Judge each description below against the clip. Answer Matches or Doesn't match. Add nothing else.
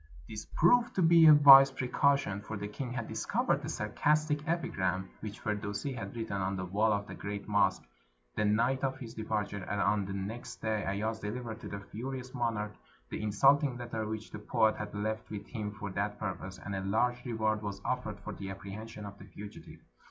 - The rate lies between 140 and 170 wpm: Doesn't match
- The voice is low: Matches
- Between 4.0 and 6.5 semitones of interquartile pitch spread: Doesn't match